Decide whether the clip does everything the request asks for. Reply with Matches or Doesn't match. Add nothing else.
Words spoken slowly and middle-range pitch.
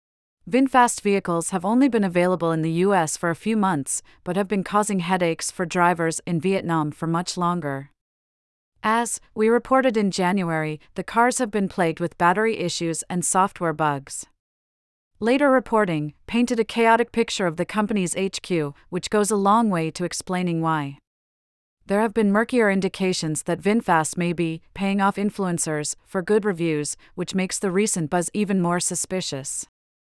Doesn't match